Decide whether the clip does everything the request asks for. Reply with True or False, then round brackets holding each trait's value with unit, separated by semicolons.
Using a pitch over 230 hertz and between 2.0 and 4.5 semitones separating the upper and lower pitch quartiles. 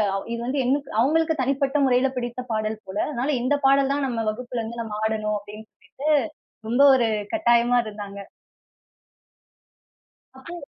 True (245 Hz; 3.8 semitones)